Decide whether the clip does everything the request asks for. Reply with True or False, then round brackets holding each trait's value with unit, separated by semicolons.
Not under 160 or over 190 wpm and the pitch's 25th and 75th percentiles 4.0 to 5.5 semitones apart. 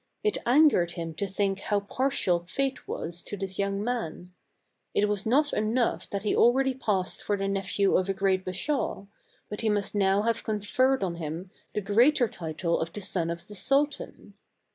True (185 wpm; 4.3 semitones)